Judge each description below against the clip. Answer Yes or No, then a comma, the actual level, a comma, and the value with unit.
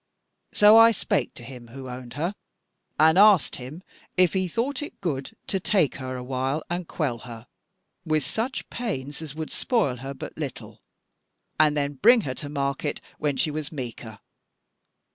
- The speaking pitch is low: No, medium, 150 Hz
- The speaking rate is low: No, average, 170 wpm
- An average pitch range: No, wide, 6.2 semitones